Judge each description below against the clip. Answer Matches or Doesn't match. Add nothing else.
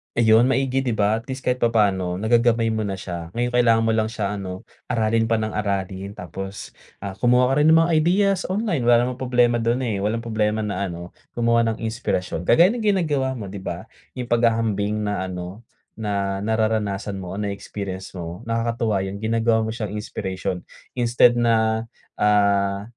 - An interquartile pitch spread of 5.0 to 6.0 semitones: Doesn't match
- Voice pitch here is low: Matches